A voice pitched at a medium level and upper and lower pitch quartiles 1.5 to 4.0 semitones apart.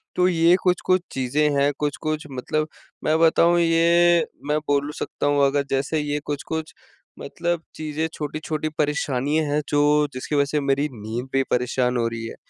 Yes: medium, 150 Hz; narrow, 2.5 semitones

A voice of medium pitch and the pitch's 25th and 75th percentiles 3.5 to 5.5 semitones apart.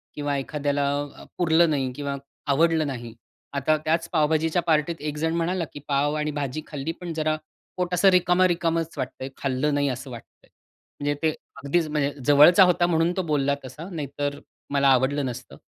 No: medium, 150 Hz; average, 2.9 semitones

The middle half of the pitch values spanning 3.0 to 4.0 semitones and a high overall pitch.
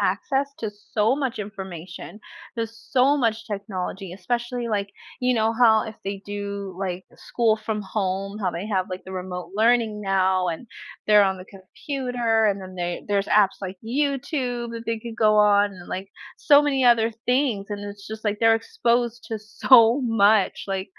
Yes: average, 3.3 semitones; high, 215 Hz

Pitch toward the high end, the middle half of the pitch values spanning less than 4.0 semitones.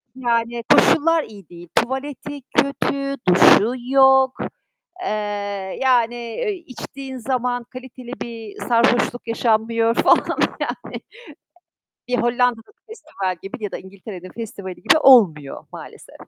Yes: high, 240 Hz; average, 3.1 semitones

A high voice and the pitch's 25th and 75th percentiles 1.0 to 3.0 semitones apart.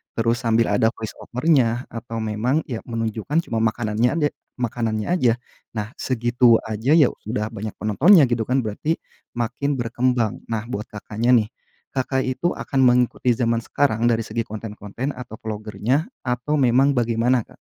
No: low, 120 Hz; narrow, 2.6 semitones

